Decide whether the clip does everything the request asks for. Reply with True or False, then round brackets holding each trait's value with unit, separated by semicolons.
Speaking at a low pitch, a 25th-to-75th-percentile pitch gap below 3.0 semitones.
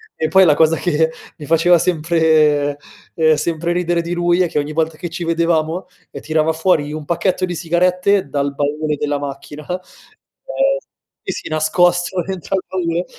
False (165 Hz; 2.4 semitones)